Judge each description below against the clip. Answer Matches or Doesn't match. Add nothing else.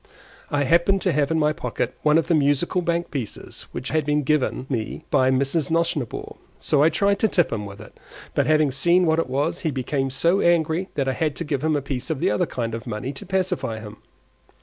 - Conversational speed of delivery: Doesn't match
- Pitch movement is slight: Doesn't match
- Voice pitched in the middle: Matches